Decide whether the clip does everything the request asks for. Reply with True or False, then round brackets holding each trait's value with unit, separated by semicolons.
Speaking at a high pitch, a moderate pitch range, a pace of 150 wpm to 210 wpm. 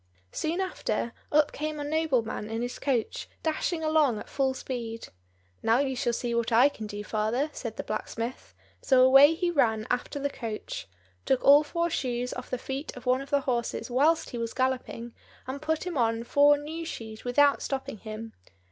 True (260 Hz; 4.0 semitones; 190 wpm)